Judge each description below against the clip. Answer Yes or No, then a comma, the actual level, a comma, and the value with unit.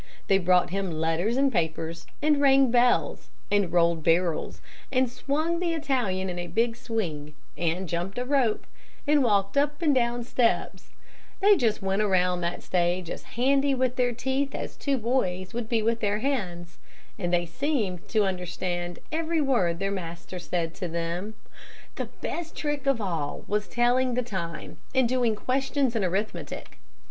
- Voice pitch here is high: Yes, high, 215 Hz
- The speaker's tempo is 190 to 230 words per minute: No, average, 165 wpm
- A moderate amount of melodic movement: No, wide, 6.7 semitones